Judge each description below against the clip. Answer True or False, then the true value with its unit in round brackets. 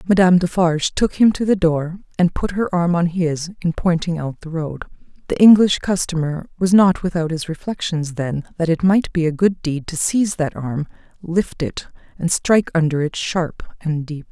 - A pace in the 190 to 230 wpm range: True (195 wpm)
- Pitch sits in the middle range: True (170 Hz)